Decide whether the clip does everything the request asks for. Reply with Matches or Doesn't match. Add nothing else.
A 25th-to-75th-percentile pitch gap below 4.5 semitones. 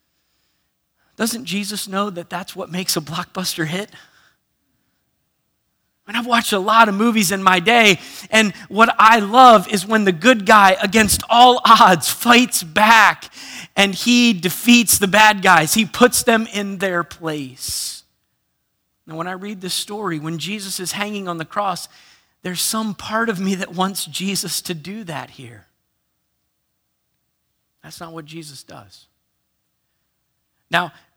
Doesn't match